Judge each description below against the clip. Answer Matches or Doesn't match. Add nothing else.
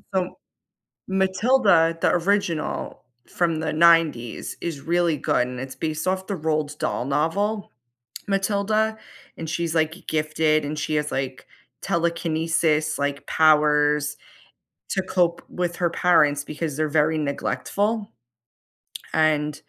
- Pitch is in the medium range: Matches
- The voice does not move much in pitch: Doesn't match